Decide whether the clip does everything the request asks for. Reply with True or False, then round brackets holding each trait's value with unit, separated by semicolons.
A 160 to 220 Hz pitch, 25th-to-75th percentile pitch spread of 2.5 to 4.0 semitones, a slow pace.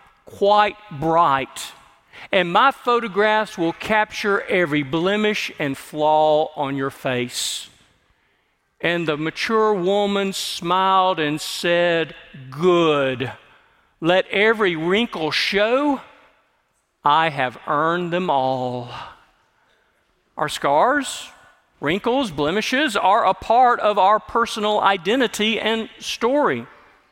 False (185 Hz; 5.5 semitones; 95 wpm)